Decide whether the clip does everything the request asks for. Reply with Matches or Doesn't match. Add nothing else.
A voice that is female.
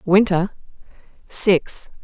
Matches